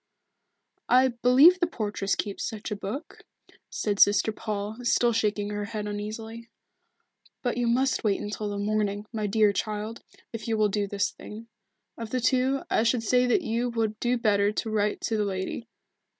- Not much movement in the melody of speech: Yes, narrow, 2.3 semitones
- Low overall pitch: No, high, 215 Hz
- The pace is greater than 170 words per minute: Yes, average, 180 wpm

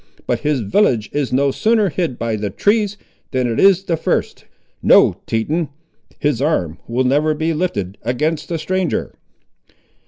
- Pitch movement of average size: No, wide, 6.5 semitones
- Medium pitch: Yes, medium, 150 Hz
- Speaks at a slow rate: No, average, 155 wpm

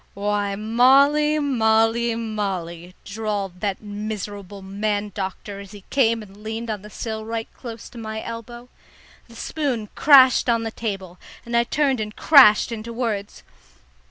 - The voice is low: No, high, 220 Hz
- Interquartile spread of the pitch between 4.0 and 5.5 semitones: No, narrow, 2.6 semitones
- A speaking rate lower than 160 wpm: Yes, average, 150 wpm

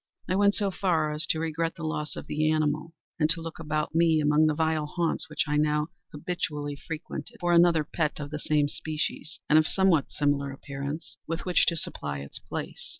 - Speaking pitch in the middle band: Yes, medium, 155 Hz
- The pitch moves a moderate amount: No, narrow, 1.8 semitones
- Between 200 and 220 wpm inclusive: Yes, fast, 205 wpm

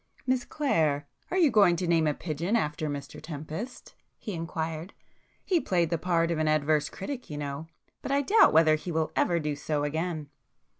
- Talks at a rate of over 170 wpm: Yes, average, 180 wpm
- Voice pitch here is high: No, medium, 160 Hz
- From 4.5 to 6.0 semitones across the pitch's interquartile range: No, average, 3.3 semitones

